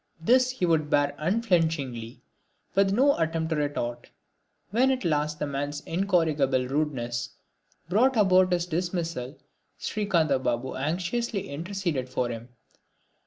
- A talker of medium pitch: Yes, medium, 160 Hz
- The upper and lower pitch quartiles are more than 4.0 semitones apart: Yes, wide, 5.4 semitones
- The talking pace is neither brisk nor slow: No, slow, 120 wpm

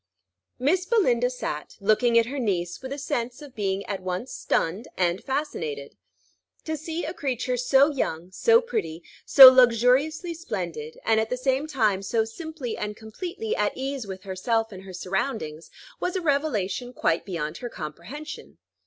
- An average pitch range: No, wide, 6.9 semitones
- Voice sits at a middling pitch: No, high, 240 Hz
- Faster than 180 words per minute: No, average, 160 wpm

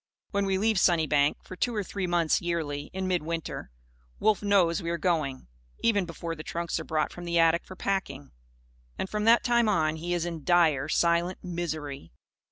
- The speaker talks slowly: No, average, 185 wpm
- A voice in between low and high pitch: Yes, medium, 170 Hz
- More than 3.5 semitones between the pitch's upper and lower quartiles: No, average, 3.1 semitones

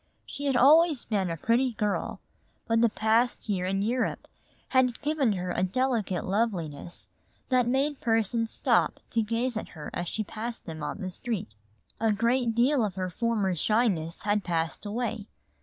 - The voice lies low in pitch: No, high, 225 Hz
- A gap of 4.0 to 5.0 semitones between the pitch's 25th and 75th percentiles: Yes, average, 4.4 semitones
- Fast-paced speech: No, average, 170 wpm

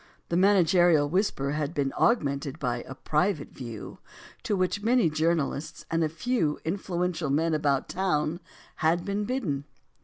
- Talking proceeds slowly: No, average, 145 wpm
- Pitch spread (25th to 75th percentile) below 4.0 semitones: No, average, 4.3 semitones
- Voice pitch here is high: No, medium, 165 Hz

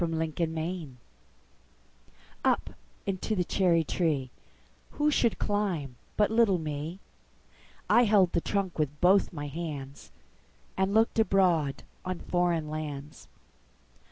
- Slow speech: Yes, slow, 105 wpm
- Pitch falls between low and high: Yes, medium, 170 Hz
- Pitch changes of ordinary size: Yes, average, 4.3 semitones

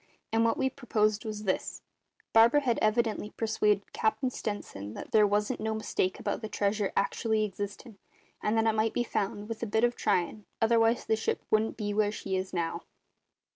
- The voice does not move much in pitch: Yes, narrow, 1.6 semitones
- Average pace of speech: Yes, average, 185 wpm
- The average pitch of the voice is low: No, high, 215 Hz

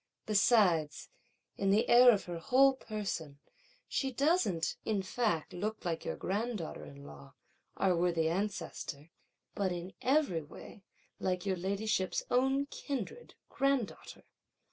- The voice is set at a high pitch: Yes, high, 195 Hz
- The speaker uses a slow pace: Yes, slow, 125 wpm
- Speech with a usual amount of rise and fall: No, wide, 6.1 semitones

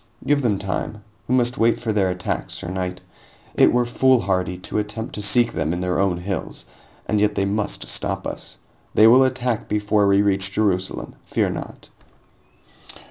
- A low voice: Yes, low, 105 Hz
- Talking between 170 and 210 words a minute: Yes, average, 175 wpm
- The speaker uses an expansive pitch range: No, average, 3.7 semitones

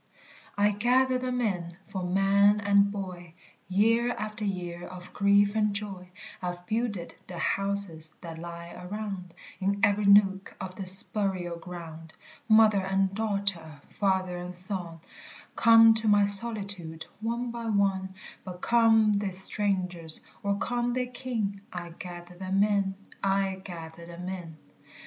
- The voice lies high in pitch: Yes, high, 195 Hz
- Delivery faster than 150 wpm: No, average, 140 wpm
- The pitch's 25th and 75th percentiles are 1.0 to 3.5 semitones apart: Yes, average, 2.8 semitones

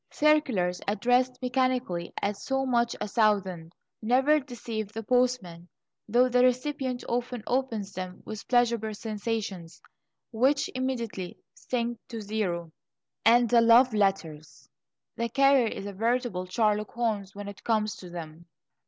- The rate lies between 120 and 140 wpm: Yes, slow, 135 wpm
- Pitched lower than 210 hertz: No, high, 225 Hz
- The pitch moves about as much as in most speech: Yes, average, 4.0 semitones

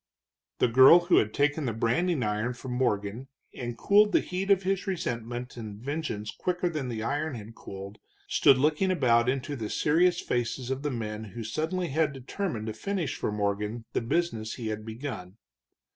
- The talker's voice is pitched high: No, low, 125 Hz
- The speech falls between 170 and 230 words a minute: Yes, average, 180 wpm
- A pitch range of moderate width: No, wide, 6.3 semitones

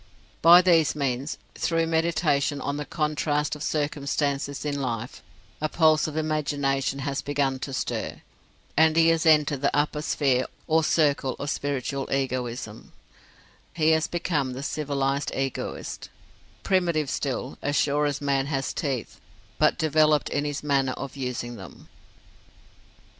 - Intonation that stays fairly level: Yes, narrow, 2.3 semitones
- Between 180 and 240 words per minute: No, average, 140 wpm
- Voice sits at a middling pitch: Yes, medium, 145 Hz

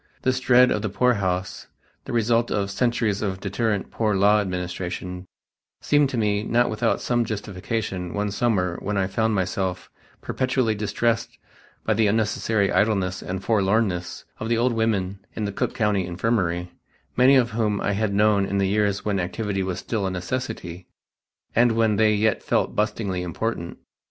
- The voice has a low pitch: Yes, low, 105 Hz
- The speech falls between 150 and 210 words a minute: Yes, average, 165 wpm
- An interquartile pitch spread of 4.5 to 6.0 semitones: No, average, 3.0 semitones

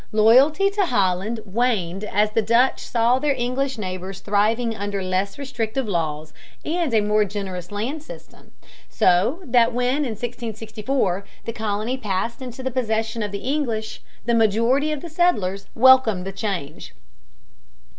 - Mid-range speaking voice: No, high, 225 Hz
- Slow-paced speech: No, average, 145 wpm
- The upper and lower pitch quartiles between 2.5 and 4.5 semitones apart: Yes, average, 4.2 semitones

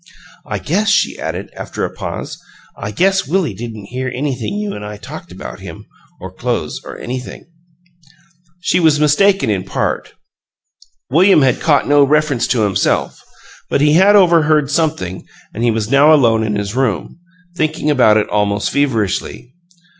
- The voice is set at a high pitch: No, medium, 140 Hz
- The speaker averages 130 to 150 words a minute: No, average, 160 wpm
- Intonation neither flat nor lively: No, wide, 6.1 semitones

